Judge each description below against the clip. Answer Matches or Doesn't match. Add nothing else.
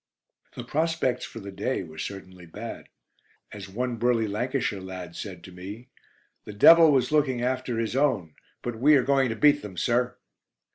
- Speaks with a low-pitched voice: Matches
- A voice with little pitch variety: Doesn't match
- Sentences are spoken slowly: Doesn't match